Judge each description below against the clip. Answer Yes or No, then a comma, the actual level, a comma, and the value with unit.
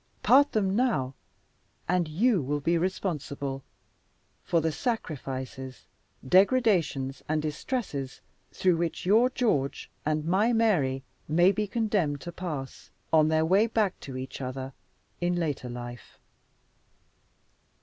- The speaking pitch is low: No, medium, 165 Hz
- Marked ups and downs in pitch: Yes, wide, 6.5 semitones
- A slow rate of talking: Yes, slow, 120 wpm